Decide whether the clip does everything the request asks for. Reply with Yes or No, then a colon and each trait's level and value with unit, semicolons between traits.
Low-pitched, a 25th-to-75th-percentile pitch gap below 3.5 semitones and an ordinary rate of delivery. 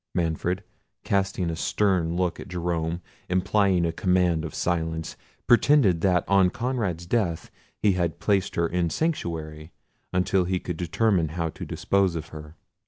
Yes: very low, 90 Hz; average, 2.8 semitones; average, 150 wpm